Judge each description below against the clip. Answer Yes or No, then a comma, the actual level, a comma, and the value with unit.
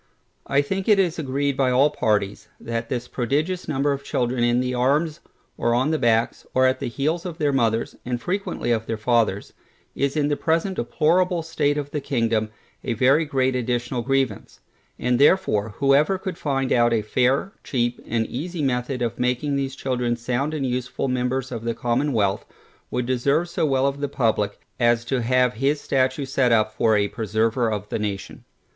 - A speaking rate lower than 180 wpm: No, average, 190 wpm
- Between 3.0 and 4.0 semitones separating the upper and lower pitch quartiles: Yes, average, 3.4 semitones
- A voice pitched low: Yes, low, 130 Hz